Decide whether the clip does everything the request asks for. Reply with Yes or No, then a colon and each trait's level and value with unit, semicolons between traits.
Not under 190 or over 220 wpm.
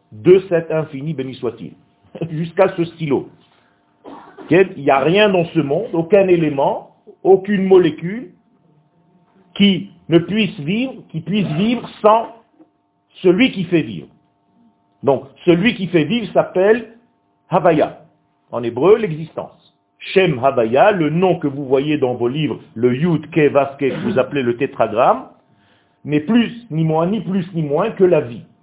No: slow, 145 wpm